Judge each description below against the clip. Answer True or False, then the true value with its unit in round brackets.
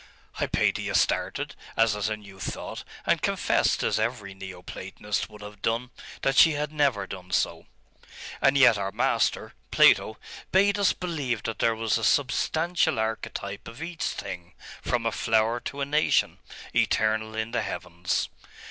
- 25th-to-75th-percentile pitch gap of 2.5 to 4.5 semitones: False (5.0 semitones)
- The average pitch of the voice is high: False (115 Hz)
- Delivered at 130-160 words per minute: True (155 wpm)